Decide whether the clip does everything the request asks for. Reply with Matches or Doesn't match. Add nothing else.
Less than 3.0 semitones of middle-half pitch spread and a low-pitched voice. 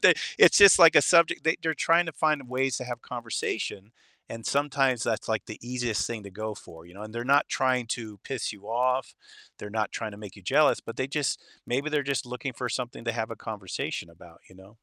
Doesn't match